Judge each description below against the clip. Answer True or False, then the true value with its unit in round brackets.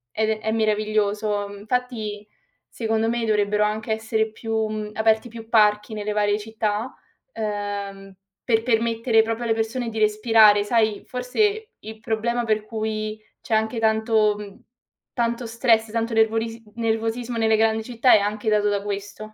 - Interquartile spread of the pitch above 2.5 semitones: False (1.2 semitones)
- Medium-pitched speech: False (220 Hz)